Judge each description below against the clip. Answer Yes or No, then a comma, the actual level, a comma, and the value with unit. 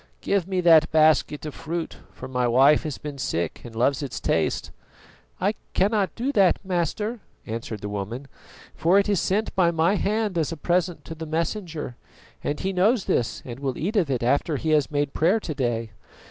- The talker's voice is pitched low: No, medium, 160 Hz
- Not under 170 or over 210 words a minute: Yes, average, 195 wpm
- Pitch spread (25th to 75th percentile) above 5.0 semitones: Yes, wide, 5.6 semitones